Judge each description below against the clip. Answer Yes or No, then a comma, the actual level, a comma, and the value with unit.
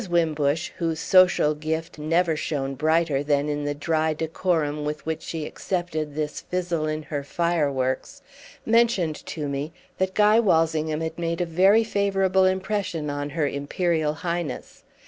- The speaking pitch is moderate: Yes, medium, 160 Hz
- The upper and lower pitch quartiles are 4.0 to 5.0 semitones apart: No, average, 2.9 semitones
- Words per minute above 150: No, average, 145 wpm